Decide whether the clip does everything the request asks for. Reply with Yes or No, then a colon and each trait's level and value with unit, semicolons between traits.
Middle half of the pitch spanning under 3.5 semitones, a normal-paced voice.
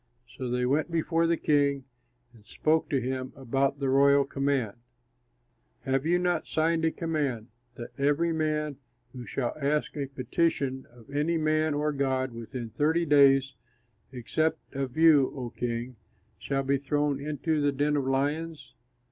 Yes: average, 2.8 semitones; average, 155 wpm